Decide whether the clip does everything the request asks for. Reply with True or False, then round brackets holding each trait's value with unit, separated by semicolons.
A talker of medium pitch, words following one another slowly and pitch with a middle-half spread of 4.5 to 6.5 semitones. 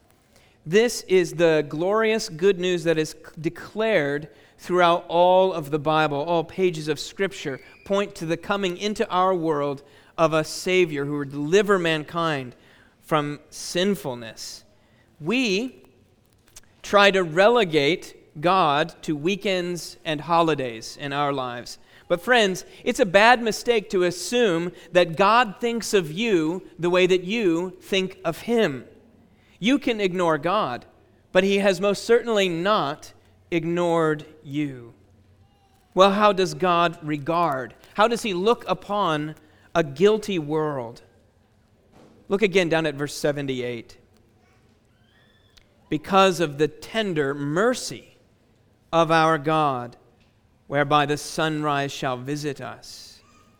True (165 Hz; 125 wpm; 5.2 semitones)